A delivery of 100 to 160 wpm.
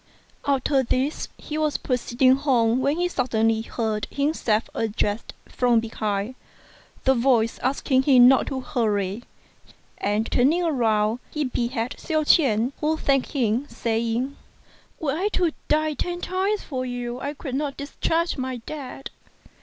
Yes: average, 140 wpm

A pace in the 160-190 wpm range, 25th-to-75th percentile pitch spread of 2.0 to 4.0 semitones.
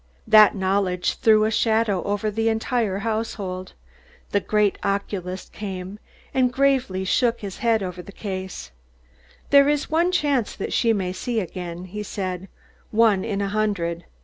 No: average, 150 wpm; average, 3.2 semitones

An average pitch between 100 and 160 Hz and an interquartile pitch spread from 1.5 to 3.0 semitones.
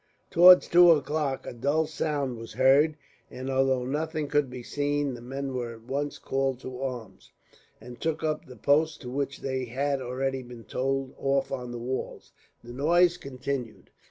Yes: low, 135 Hz; narrow, 2.6 semitones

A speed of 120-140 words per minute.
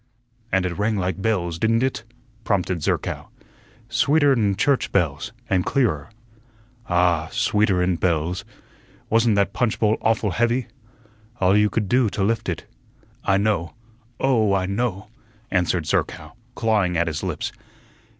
Yes: slow, 135 wpm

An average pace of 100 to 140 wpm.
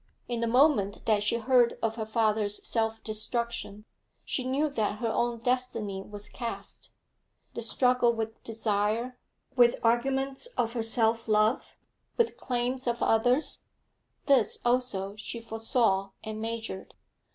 Yes: slow, 135 wpm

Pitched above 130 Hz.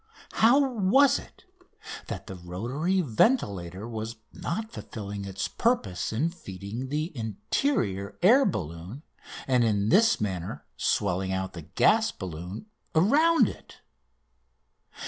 No: low, 115 Hz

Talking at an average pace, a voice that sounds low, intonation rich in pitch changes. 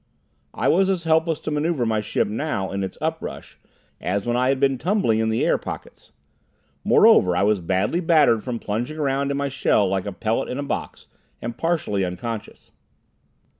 Yes: average, 190 wpm; low, 120 Hz; wide, 6.8 semitones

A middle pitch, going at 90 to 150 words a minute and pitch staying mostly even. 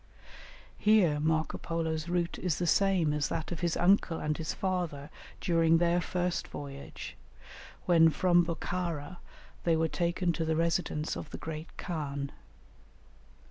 Yes: medium, 165 Hz; average, 140 wpm; narrow, 2.0 semitones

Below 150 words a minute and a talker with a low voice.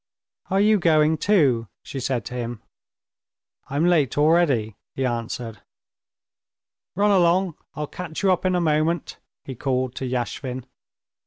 No: average, 140 wpm; medium, 150 Hz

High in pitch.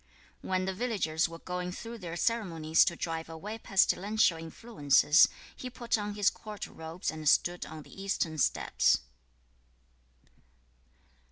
No: medium, 180 Hz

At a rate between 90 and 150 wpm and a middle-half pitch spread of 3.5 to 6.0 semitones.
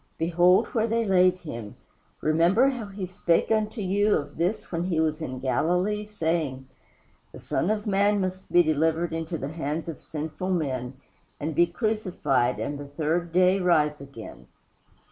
No: average, 165 wpm; average, 4.1 semitones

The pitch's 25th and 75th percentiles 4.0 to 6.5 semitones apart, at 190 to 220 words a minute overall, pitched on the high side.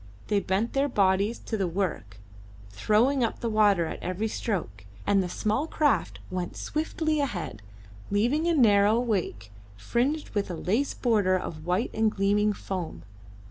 No: average, 4.4 semitones; average, 160 wpm; high, 205 Hz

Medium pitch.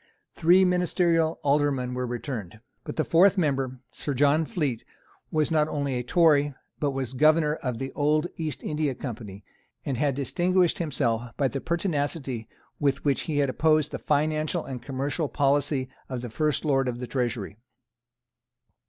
Yes: medium, 145 Hz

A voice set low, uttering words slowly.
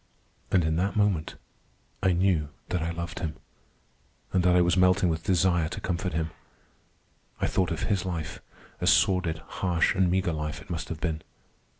No: very low, 85 Hz; average, 180 wpm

